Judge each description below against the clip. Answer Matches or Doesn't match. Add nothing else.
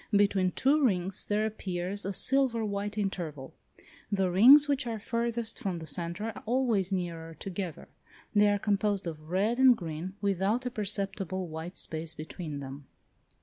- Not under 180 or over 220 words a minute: Doesn't match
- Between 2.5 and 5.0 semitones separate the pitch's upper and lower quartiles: Matches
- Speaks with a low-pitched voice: Doesn't match